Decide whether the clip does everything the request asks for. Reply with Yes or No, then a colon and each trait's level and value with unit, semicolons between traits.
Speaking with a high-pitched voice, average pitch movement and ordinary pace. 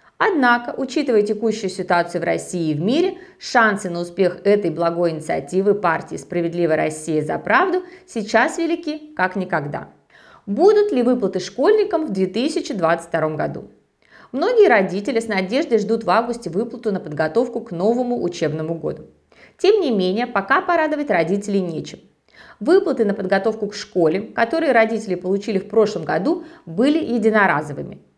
No: high, 215 Hz; wide, 7.7 semitones; average, 140 wpm